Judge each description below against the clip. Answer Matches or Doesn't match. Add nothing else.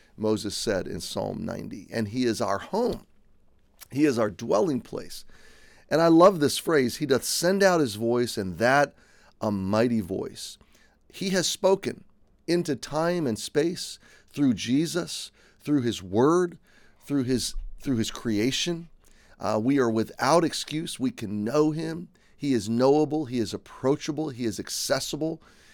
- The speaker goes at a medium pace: Matches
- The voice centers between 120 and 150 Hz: Matches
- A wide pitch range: Matches